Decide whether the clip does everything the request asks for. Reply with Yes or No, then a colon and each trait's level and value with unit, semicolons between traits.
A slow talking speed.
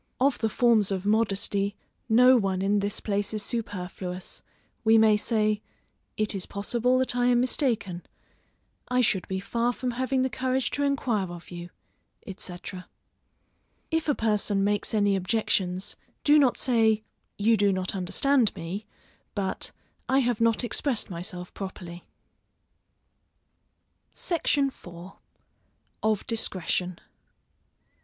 Yes: slow, 130 wpm